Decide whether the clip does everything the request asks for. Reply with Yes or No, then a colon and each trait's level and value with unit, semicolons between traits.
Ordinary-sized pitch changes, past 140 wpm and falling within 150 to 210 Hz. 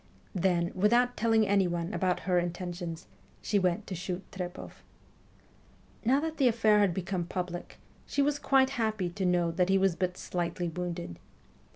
Yes: average, 3.5 semitones; average, 160 wpm; medium, 185 Hz